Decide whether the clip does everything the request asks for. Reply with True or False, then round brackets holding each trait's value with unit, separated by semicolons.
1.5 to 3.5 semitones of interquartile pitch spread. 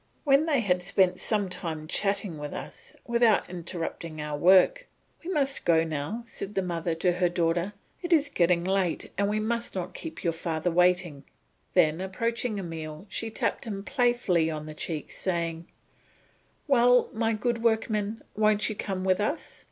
False (5.0 semitones)